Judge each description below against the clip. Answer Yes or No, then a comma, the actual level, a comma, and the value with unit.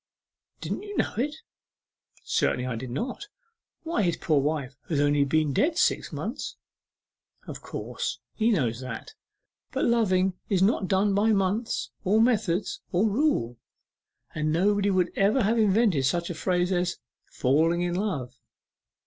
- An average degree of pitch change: No, wide, 5.9 semitones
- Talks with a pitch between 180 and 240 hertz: Yes, medium, 185 Hz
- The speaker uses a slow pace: No, average, 150 wpm